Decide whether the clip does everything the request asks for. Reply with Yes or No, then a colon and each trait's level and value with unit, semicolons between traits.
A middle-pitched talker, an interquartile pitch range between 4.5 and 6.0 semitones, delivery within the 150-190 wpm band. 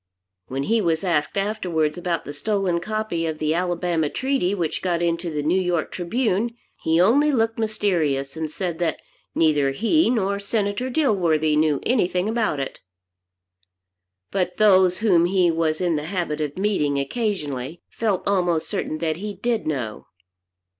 Yes: medium, 175 Hz; average, 4.8 semitones; average, 155 wpm